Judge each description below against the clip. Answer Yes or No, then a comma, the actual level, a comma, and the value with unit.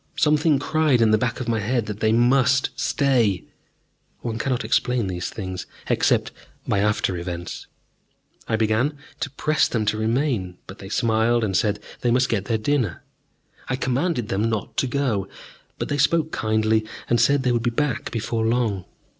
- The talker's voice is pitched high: No, low, 115 Hz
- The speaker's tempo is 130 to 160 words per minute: No, average, 175 wpm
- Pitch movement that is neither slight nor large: Yes, average, 3.4 semitones